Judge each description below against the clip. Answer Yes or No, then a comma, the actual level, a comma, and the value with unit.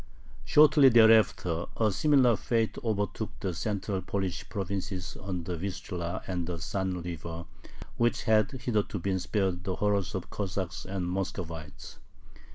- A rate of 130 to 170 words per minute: Yes, average, 140 wpm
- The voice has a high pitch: No, very low, 95 Hz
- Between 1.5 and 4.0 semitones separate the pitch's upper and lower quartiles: Yes, average, 3.3 semitones